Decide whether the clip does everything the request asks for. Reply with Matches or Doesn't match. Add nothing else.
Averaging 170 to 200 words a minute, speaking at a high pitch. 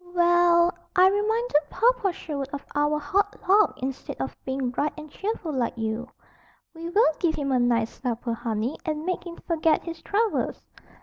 Matches